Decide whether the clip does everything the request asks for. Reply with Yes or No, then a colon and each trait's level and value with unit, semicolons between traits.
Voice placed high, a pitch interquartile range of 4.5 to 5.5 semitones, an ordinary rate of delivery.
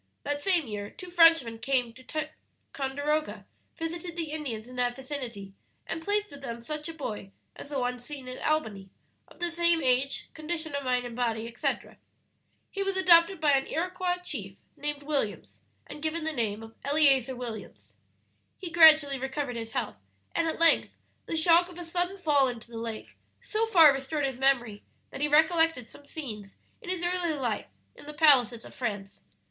Yes: very high, 285 Hz; average, 5.2 semitones; average, 180 wpm